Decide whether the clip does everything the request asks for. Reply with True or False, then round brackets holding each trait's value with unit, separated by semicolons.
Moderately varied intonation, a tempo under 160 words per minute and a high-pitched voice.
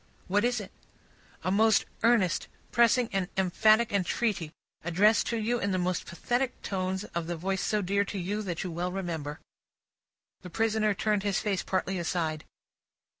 False (3.2 semitones; 165 wpm; 195 Hz)